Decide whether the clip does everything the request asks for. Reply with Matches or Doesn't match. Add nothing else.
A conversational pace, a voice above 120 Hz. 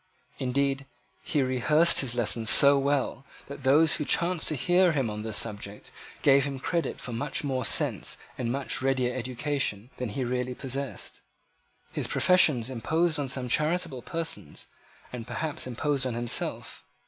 Matches